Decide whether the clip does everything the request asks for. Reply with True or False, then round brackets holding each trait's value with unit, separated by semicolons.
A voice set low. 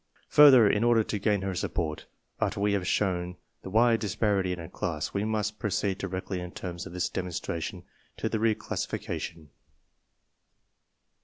True (100 Hz)